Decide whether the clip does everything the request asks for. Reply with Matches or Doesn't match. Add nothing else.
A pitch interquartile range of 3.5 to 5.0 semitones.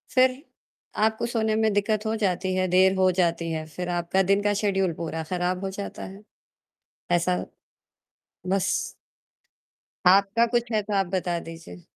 Doesn't match